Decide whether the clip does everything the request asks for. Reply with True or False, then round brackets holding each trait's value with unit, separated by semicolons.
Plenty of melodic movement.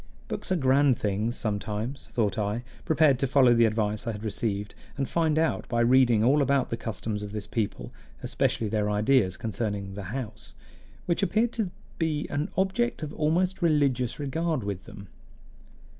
True (6.1 semitones)